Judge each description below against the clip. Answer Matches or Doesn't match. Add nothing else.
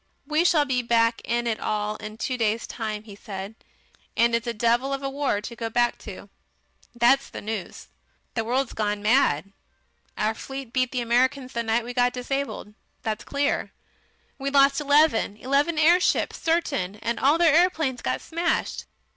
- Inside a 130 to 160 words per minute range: Doesn't match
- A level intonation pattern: Doesn't match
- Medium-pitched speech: Doesn't match